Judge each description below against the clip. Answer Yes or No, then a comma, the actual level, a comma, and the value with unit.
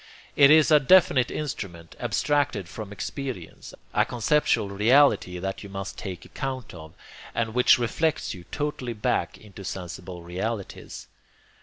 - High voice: No, low, 110 Hz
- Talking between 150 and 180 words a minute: No, slow, 135 wpm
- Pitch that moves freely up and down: Yes, wide, 6.3 semitones